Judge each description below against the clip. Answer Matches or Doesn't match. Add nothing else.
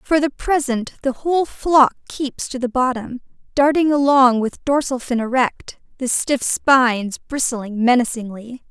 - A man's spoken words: Doesn't match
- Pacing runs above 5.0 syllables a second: Doesn't match